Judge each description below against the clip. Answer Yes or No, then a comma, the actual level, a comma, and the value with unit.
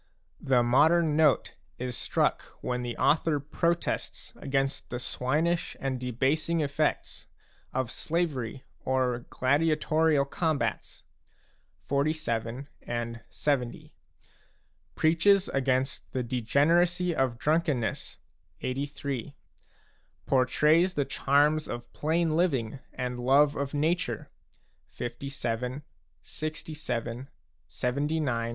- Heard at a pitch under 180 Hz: Yes, medium, 140 Hz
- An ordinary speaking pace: No, slow, 90 wpm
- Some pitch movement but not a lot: Yes, average, 3.9 semitones